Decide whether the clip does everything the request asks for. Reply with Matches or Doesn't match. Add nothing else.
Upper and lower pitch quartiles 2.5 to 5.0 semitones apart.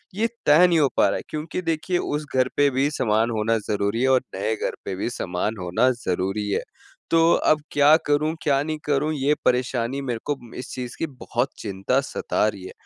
Doesn't match